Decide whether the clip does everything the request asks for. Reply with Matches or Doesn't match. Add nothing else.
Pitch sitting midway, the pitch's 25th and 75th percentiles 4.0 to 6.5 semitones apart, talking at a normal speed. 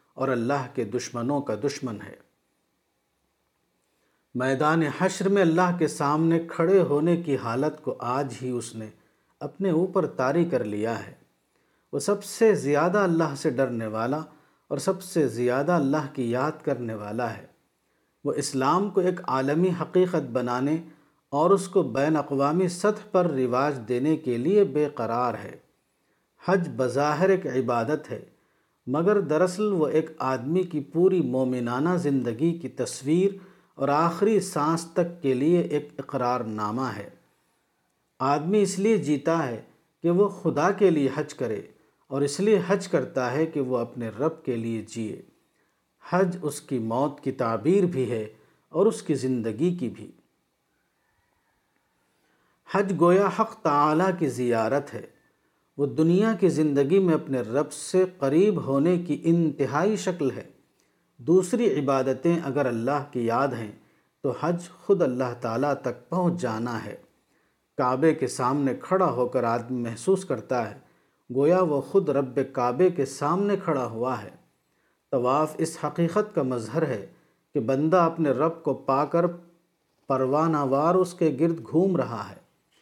Matches